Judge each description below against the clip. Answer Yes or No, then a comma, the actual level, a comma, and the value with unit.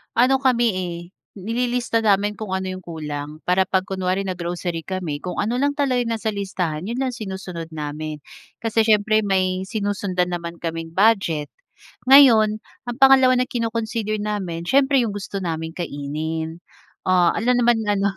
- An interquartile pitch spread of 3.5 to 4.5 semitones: No, average, 4.9 semitones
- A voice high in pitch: Yes, high, 195 Hz